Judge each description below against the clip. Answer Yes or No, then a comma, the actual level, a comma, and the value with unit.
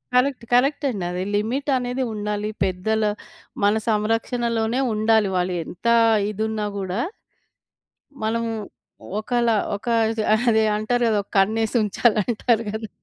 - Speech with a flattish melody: Yes, narrow, 2.3 semitones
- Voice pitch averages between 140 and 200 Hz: No, high, 220 Hz